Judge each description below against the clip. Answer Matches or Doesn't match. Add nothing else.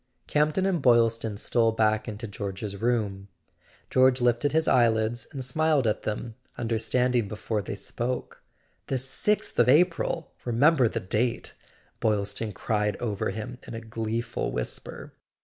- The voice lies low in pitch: Matches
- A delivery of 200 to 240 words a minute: Doesn't match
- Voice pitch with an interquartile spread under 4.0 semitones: Matches